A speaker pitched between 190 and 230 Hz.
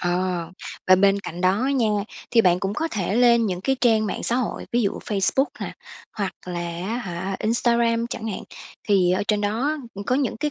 Yes: high, 210 Hz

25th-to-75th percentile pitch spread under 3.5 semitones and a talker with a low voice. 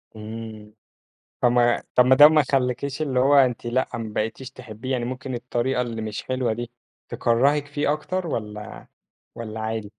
Yes: average, 2.9 semitones; low, 125 Hz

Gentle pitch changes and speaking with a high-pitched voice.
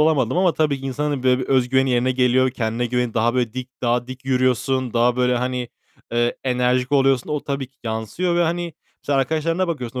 No: narrow, 2.2 semitones; low, 130 Hz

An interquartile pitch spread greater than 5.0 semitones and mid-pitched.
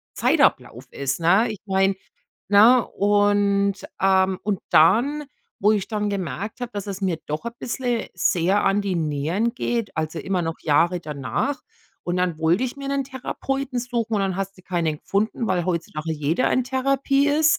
No: wide, 5.4 semitones; high, 200 Hz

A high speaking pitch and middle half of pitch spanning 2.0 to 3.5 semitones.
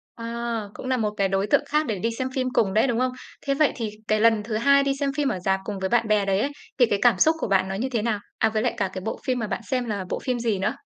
No: high, 225 Hz; average, 4.0 semitones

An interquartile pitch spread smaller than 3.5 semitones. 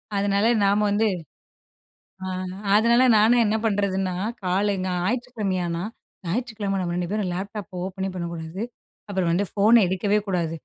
Yes: narrow, 2.6 semitones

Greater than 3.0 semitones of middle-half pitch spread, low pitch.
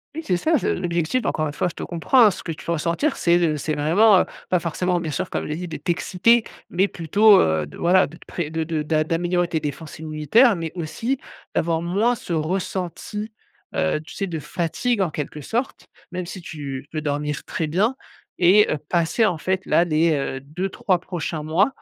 No: average, 3.4 semitones; medium, 170 Hz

